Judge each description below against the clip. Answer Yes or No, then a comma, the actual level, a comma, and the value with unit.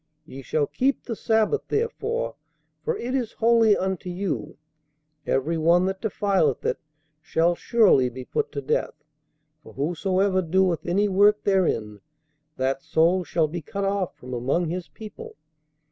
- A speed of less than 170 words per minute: Yes, average, 145 wpm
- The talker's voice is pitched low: No, medium, 185 Hz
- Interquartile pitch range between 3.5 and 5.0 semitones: Yes, average, 4.7 semitones